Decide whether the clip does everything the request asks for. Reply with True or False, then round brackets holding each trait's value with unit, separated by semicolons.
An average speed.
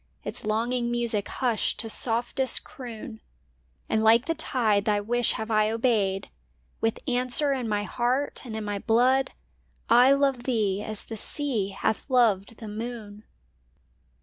True (150 wpm)